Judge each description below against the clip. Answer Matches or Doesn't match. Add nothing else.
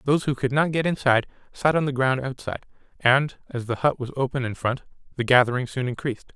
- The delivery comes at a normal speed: Doesn't match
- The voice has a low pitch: Matches